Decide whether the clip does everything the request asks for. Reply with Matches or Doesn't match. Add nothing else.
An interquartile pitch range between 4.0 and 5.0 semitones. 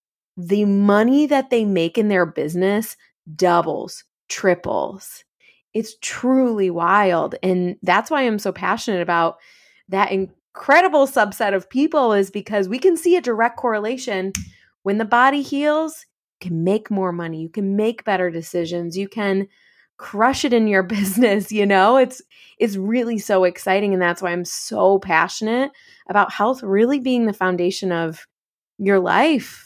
Matches